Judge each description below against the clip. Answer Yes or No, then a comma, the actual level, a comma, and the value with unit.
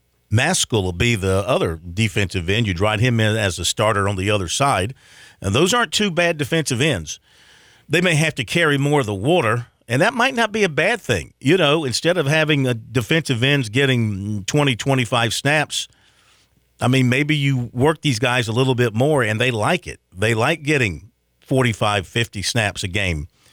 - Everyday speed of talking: Yes, average, 195 wpm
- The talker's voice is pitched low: Yes, low, 125 Hz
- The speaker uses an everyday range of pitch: No, wide, 5.8 semitones